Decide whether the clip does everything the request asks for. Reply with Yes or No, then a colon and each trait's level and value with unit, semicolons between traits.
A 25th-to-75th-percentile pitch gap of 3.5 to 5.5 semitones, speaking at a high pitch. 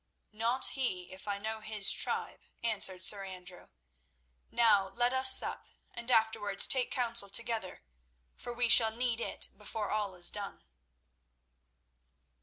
No: average, 3.1 semitones; high, 220 Hz